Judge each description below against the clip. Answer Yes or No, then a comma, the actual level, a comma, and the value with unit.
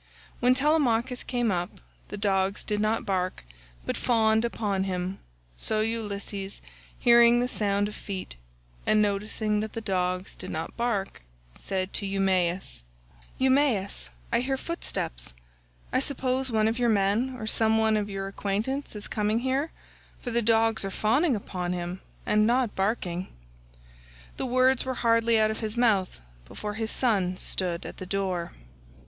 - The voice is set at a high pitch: Yes, high, 215 Hz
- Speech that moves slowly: No, average, 155 wpm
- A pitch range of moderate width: Yes, average, 3.5 semitones